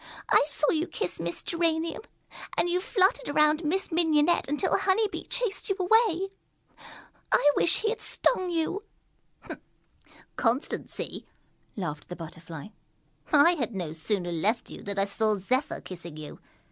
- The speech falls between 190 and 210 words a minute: No, average, 145 wpm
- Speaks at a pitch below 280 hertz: No, very high, 300 Hz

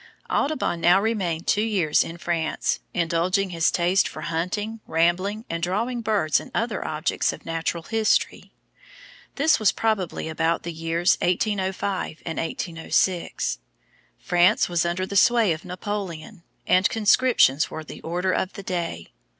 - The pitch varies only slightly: No, average, 3.7 semitones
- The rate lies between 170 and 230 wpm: No, average, 140 wpm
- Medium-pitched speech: Yes, medium, 180 Hz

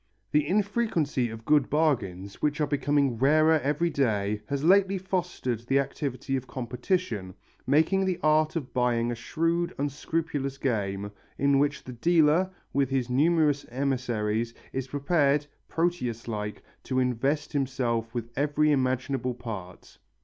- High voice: No, medium, 140 Hz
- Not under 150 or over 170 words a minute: No, slow, 135 wpm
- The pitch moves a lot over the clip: No, average, 4.3 semitones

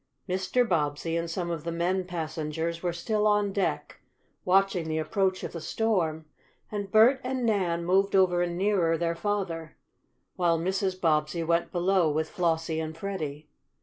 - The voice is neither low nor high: Yes, medium, 175 Hz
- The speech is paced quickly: No, average, 155 wpm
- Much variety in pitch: No, average, 3.1 semitones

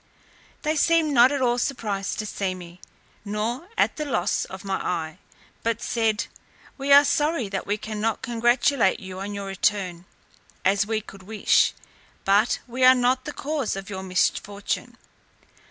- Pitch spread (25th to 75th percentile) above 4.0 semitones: Yes, average, 4.6 semitones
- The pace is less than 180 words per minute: Yes, average, 160 wpm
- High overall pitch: Yes, high, 215 Hz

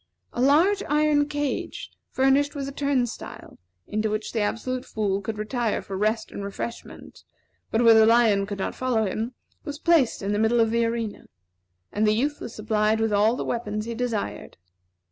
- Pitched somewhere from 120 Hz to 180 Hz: No, high, 230 Hz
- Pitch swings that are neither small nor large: Yes, average, 3.6 semitones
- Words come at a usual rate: Yes, average, 185 wpm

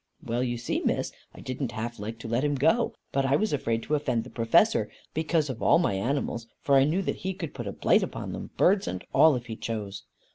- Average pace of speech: No, fast, 245 wpm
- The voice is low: Yes, low, 130 Hz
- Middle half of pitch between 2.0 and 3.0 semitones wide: No, average, 4.5 semitones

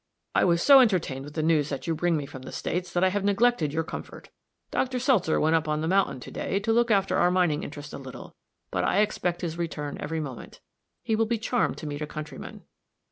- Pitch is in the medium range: Yes, medium, 170 Hz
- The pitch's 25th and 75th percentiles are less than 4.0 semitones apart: No, average, 5.0 semitones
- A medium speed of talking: No, fast, 240 wpm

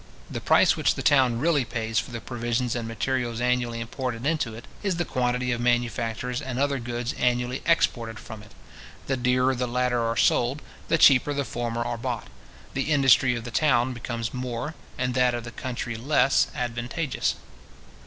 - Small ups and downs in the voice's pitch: Yes, narrow, 1.8 semitones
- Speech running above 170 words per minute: Yes, average, 180 wpm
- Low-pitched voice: Yes, low, 125 Hz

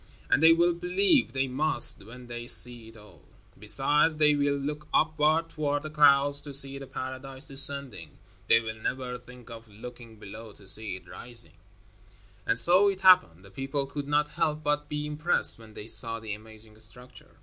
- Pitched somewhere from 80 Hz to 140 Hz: Yes, low, 135 Hz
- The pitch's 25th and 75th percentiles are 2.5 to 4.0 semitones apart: No, average, 4.7 semitones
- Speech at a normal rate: Yes, average, 180 wpm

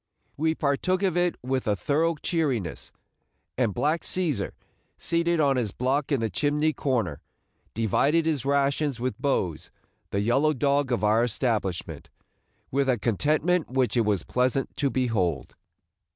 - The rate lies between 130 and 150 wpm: Yes, average, 145 wpm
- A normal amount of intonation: Yes, average, 4.9 semitones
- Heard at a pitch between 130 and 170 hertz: Yes, low, 135 Hz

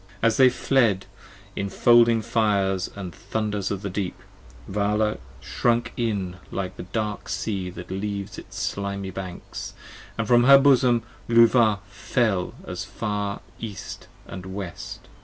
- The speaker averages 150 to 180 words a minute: No, average, 140 wpm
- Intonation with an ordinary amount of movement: Yes, average, 3.2 semitones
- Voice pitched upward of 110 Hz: No, low, 105 Hz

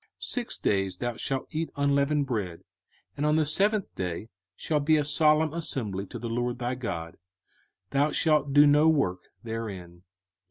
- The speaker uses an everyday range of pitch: No, wide, 5.9 semitones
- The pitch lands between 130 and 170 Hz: Yes, medium, 140 Hz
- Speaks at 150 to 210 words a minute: Yes, average, 165 wpm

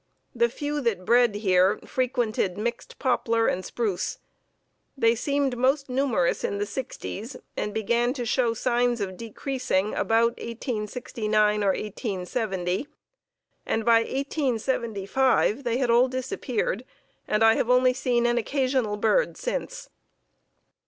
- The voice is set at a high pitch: Yes, high, 235 Hz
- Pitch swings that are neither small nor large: Yes, average, 3.3 semitones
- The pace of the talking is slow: Yes, slow, 125 wpm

